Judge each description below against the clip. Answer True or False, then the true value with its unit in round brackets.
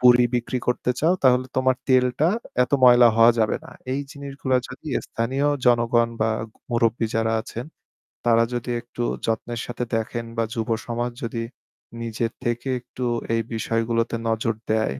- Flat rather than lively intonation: True (1.6 semitones)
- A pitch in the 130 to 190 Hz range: False (120 Hz)